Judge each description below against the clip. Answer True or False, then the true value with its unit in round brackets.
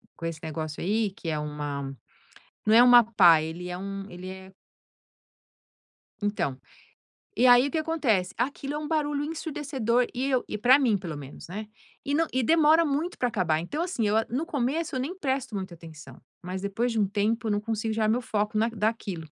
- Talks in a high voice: True (220 Hz)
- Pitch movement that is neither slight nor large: False (6.4 semitones)